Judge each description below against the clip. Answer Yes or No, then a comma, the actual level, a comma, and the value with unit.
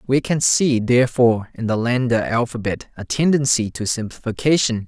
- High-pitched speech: No, low, 120 Hz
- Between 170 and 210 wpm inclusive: No, average, 150 wpm